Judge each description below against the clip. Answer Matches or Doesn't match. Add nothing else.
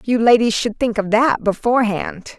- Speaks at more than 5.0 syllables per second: Doesn't match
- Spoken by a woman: Matches